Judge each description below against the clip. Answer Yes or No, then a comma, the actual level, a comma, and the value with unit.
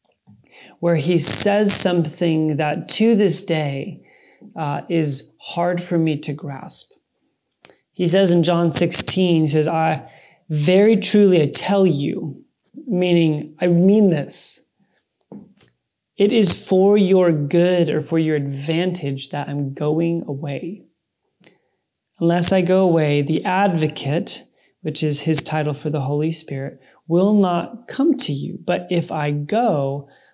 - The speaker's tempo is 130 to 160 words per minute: Yes, slow, 135 wpm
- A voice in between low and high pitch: Yes, medium, 170 Hz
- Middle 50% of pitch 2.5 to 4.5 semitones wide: Yes, average, 3.6 semitones